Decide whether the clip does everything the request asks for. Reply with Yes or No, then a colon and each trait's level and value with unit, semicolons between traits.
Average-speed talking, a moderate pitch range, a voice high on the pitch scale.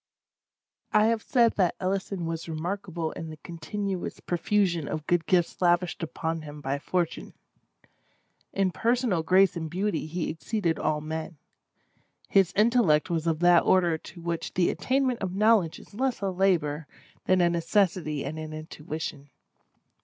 No: average, 150 wpm; average, 3.6 semitones; medium, 175 Hz